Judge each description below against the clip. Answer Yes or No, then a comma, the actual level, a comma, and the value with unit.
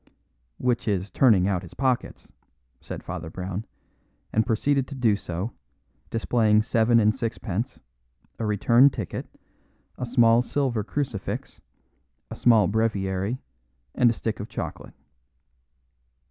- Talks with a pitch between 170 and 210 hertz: No, low, 110 Hz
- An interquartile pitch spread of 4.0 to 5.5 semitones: No, average, 3.4 semitones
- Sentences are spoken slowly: Yes, slow, 120 wpm